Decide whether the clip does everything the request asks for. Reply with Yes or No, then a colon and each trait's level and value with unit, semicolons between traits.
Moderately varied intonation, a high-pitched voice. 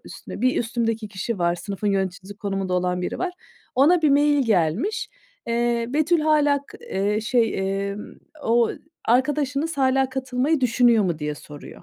No: wide, 6.2 semitones; high, 235 Hz